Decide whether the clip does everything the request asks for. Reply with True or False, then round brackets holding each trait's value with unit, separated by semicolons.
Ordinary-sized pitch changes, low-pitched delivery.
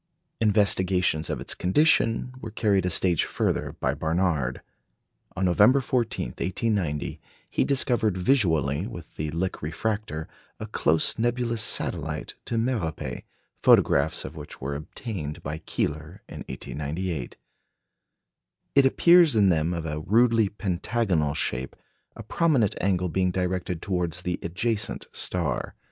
False (6.0 semitones; 95 Hz)